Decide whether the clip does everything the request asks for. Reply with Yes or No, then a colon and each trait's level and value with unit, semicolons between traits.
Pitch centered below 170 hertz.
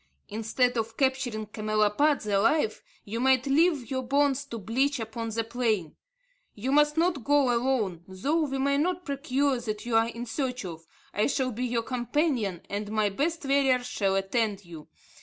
No: high, 245 Hz